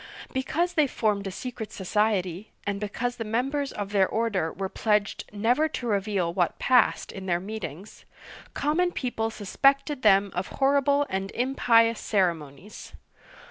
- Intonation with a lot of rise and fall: No, average, 4.8 semitones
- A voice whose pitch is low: No, high, 215 Hz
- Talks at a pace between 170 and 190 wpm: No, average, 145 wpm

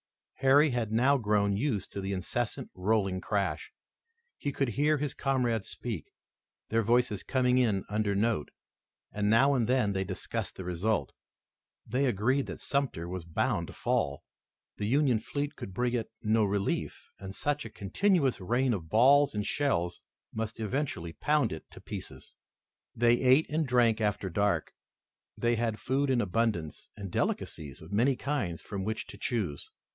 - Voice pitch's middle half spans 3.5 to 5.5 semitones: Yes, average, 4.8 semitones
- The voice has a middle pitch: No, low, 115 Hz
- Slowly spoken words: No, average, 165 wpm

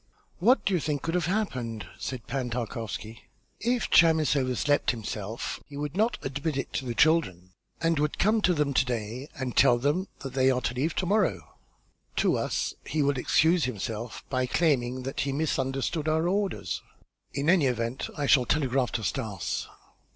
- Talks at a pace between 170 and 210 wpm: Yes, average, 180 wpm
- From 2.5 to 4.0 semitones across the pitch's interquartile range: No, average, 4.6 semitones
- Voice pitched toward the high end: No, low, 135 Hz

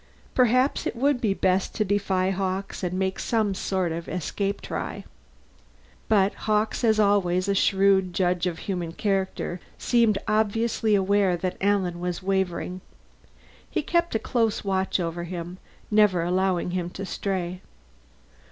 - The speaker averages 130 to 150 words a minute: Yes, average, 145 wpm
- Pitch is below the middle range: No, high, 190 Hz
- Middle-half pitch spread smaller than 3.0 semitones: Yes, narrow, 2.5 semitones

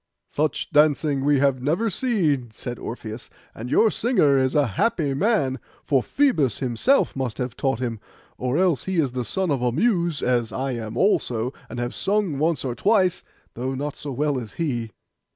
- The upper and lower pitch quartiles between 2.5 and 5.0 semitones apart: No, wide, 5.4 semitones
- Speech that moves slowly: No, average, 185 wpm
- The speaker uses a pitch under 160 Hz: Yes, medium, 140 Hz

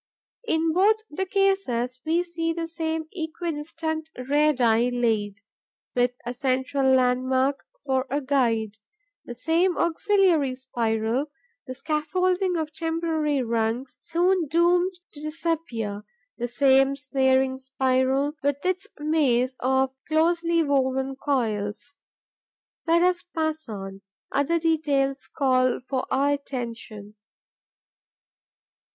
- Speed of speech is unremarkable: No, slow, 105 wpm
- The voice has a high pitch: Yes, very high, 280 Hz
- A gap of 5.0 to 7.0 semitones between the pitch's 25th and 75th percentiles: No, average, 4.3 semitones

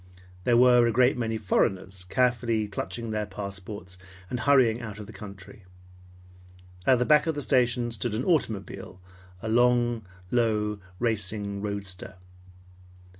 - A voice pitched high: No, low, 110 Hz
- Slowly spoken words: Yes, slow, 130 wpm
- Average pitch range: Yes, average, 3.4 semitones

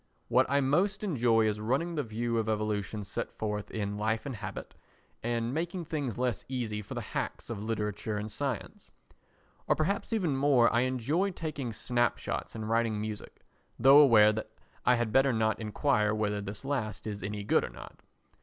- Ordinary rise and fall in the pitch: Yes, average, 4.3 semitones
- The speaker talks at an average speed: Yes, average, 180 wpm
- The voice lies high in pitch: No, low, 115 Hz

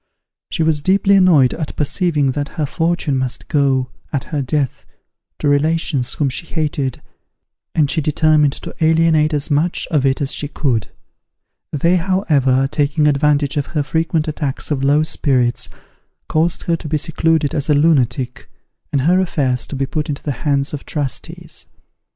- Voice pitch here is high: No, medium, 150 Hz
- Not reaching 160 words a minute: No, average, 165 wpm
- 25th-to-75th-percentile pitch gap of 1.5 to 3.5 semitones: Yes, narrow, 2.6 semitones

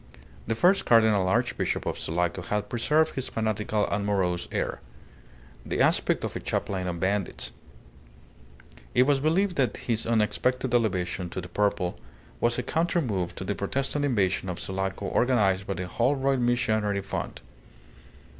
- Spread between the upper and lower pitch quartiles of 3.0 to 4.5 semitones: No, average, 5.0 semitones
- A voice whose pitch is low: Yes, low, 105 Hz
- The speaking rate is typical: Yes, average, 150 wpm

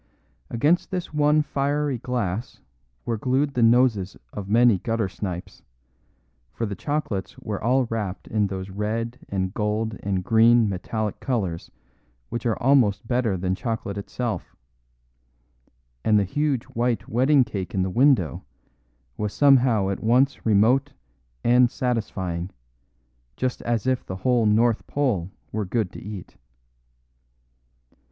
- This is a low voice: Yes, low, 115 Hz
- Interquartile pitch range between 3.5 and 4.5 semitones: Yes, average, 4.1 semitones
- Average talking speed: No, slow, 130 wpm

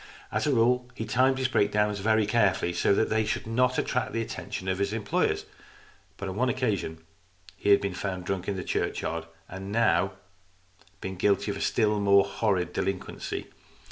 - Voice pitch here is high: No, low, 100 Hz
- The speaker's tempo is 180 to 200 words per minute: Yes, average, 190 wpm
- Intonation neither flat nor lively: Yes, average, 3.0 semitones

